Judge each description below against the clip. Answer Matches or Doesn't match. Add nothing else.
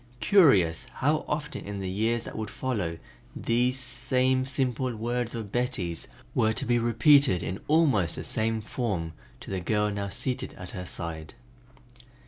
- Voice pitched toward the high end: Doesn't match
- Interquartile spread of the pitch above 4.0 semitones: Matches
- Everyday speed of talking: Matches